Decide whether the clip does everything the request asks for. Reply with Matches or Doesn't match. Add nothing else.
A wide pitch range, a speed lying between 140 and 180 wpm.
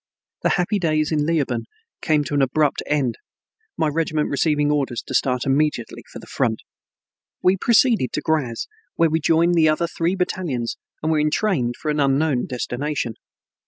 Doesn't match